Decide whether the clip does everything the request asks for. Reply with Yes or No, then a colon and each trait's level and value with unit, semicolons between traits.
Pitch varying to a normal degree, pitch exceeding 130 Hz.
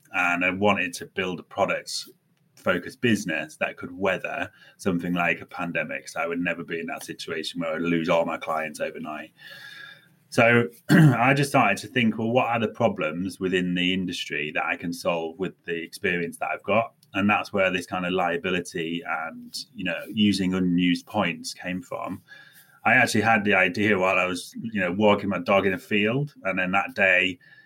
No: average, 4.1 semitones; very low, 95 Hz